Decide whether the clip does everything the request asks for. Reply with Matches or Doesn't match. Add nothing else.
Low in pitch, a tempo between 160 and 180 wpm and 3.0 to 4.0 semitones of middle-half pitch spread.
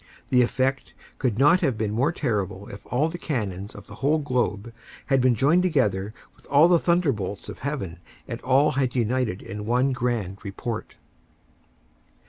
Doesn't match